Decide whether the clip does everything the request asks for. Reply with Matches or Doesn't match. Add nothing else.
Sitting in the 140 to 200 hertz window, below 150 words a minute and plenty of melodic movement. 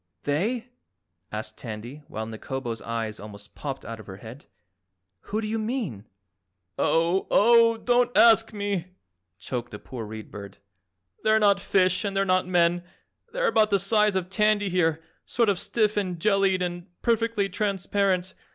Doesn't match